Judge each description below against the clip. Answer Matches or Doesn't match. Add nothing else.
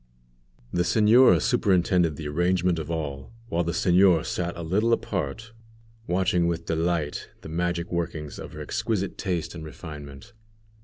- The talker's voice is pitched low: Matches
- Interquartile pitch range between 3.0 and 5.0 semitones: Doesn't match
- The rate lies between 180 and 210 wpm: Doesn't match